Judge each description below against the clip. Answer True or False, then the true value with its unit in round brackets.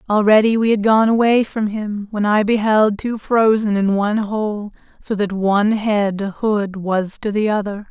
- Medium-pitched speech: False (210 Hz)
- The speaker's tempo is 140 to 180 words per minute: False (190 wpm)